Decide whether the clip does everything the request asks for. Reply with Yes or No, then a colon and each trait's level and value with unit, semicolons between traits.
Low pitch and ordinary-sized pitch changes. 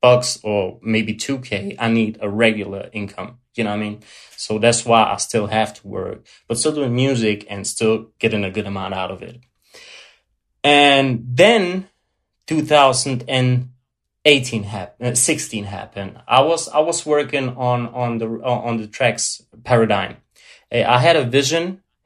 Yes: low, 120 Hz; average, 4.1 semitones